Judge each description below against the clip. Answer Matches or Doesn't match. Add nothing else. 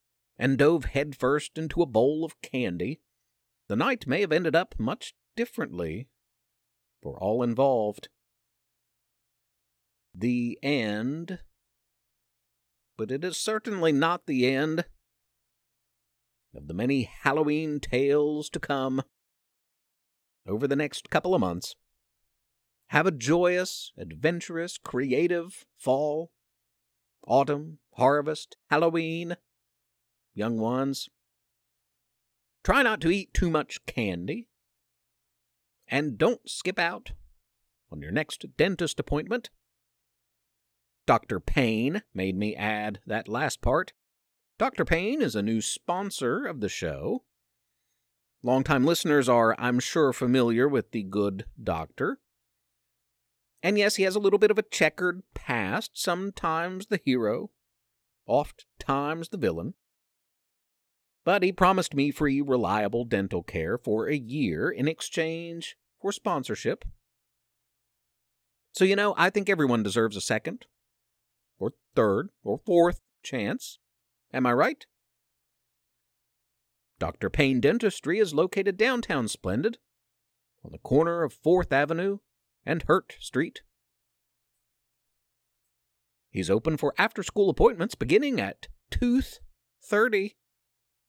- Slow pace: Matches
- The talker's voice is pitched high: Doesn't match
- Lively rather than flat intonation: Matches